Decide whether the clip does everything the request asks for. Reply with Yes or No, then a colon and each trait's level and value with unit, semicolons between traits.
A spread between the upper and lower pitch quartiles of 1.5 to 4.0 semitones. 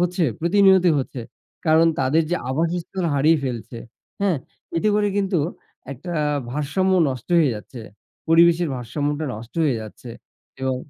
No: average, 5.2 semitones